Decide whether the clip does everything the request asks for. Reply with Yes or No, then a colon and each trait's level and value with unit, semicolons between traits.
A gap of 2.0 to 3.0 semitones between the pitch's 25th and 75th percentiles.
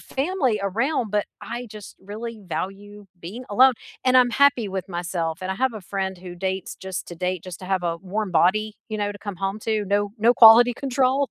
No: average, 4.1 semitones